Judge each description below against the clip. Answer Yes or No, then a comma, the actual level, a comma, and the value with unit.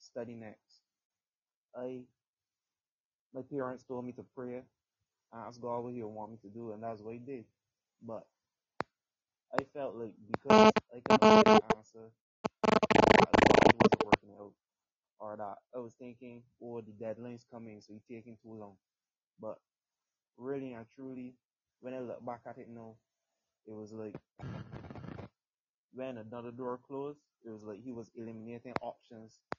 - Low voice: Yes, low, 120 Hz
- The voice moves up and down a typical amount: No, narrow, 2.3 semitones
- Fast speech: No, average, 155 wpm